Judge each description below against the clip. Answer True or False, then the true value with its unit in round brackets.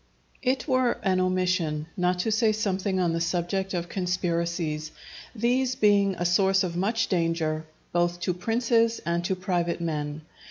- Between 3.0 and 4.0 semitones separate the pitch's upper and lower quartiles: True (3.3 semitones)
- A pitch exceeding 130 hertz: True (185 Hz)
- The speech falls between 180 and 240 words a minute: False (160 wpm)